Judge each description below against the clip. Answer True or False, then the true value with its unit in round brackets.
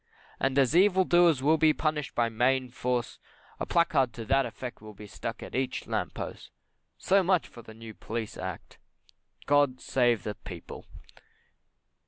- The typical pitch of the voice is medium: False (130 Hz)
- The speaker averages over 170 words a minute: False (165 wpm)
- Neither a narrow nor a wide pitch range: True (5.0 semitones)